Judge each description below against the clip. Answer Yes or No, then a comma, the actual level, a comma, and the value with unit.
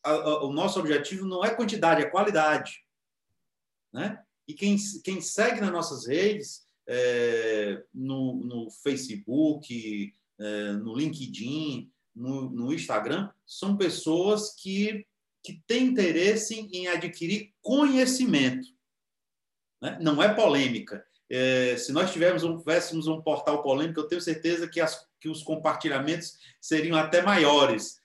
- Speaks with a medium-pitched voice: Yes, medium, 165 Hz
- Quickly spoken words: No, average, 125 wpm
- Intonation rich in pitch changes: Yes, wide, 5.9 semitones